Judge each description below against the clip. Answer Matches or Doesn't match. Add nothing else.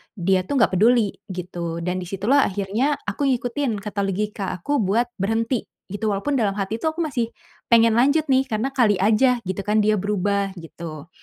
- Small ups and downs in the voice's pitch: Doesn't match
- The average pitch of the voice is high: Matches